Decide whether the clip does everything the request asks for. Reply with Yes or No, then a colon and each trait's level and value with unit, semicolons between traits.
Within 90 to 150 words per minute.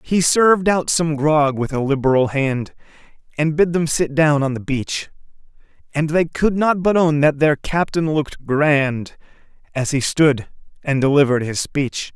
No: average, 175 wpm